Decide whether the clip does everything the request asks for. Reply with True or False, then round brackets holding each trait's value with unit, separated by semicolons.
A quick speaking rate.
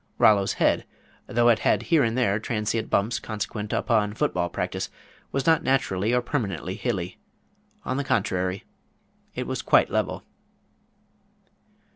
False (140 wpm)